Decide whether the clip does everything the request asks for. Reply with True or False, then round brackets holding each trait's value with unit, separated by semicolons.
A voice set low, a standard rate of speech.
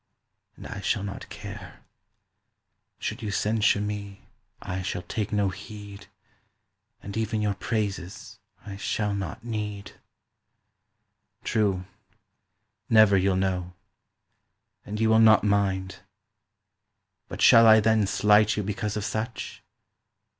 False (105 Hz; 120 wpm)